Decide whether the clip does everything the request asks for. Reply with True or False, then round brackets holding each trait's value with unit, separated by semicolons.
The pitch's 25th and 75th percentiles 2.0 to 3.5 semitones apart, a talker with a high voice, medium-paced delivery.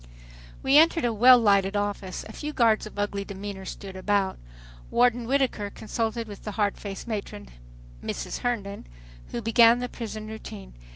True (2.9 semitones; 215 Hz; 160 wpm)